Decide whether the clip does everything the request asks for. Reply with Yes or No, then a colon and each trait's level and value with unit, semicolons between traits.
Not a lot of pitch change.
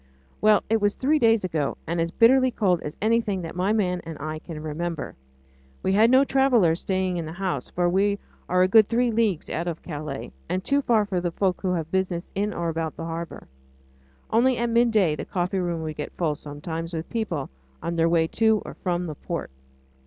No: average, 4.7 semitones